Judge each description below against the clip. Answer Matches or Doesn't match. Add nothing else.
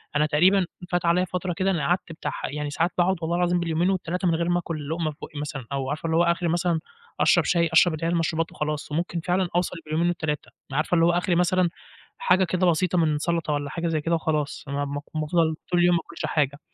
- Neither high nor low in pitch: Matches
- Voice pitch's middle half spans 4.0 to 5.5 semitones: Doesn't match